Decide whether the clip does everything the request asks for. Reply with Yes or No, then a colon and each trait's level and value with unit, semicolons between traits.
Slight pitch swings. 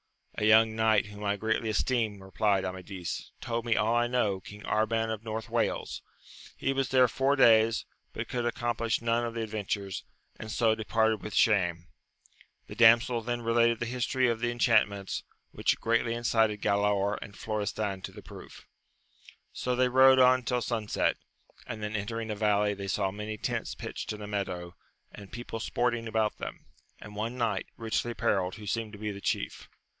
Yes: narrow, 2.2 semitones